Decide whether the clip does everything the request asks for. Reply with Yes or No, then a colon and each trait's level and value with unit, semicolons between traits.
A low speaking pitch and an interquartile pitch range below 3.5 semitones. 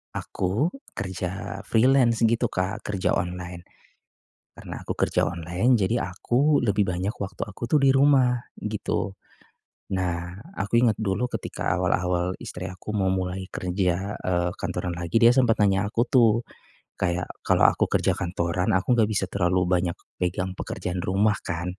No: very low, 95 Hz; average, 4.0 semitones